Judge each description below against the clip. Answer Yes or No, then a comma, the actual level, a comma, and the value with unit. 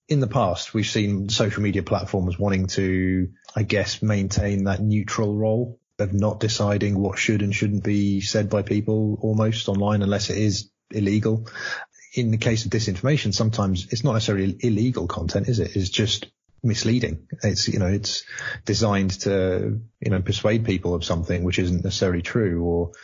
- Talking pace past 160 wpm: Yes, average, 170 wpm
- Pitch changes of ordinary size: No, narrow, 2.1 semitones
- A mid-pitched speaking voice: No, low, 105 Hz